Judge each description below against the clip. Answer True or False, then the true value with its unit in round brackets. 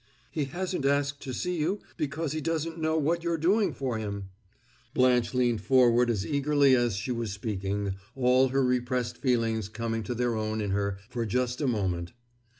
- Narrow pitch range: False (4.5 semitones)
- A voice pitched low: True (125 Hz)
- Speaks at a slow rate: False (180 wpm)